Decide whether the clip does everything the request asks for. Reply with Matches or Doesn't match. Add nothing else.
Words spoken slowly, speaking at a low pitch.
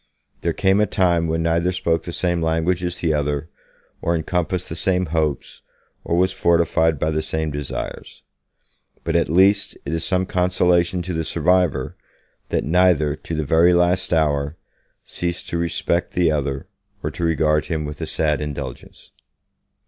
Doesn't match